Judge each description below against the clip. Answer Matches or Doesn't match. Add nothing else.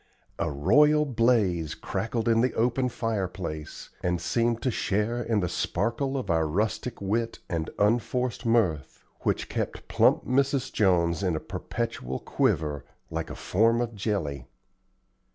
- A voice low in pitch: Matches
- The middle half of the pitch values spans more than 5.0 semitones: Matches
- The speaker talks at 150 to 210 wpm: Doesn't match